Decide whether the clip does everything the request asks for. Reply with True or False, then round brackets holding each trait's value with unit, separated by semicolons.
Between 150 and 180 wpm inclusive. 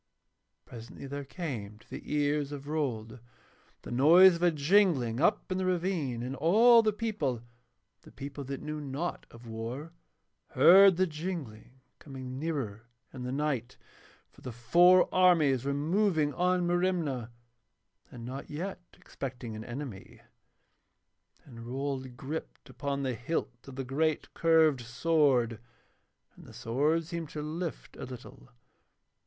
False (140 wpm)